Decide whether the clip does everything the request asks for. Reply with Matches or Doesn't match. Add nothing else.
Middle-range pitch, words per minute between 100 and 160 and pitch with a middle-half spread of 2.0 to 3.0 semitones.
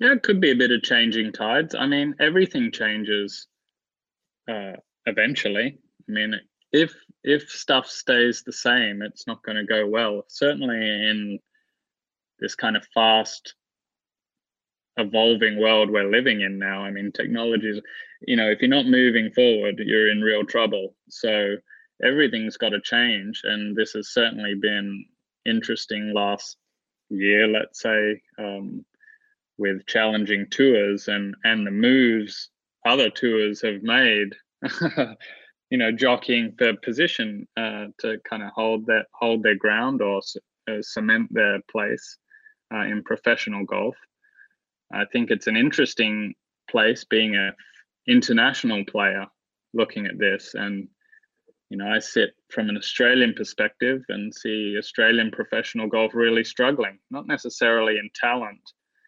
Doesn't match